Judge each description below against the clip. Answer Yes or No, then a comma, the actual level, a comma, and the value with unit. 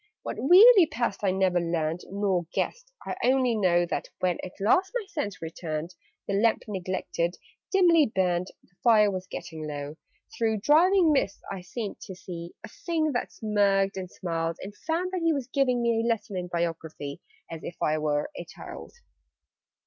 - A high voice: Yes, high, 195 Hz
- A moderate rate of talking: Yes, average, 175 wpm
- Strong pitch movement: Yes, wide, 6.7 semitones